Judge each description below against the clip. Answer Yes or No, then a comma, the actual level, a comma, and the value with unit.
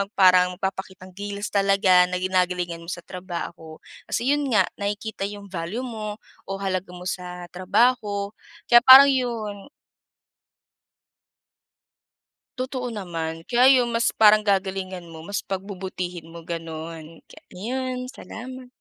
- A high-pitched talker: Yes, high, 195 Hz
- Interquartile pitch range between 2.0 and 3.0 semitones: No, average, 3.4 semitones